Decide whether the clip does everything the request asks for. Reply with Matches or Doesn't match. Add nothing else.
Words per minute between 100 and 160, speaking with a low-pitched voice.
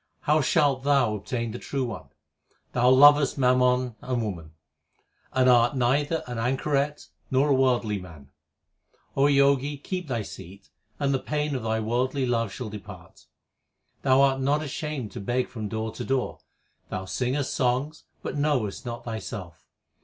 Matches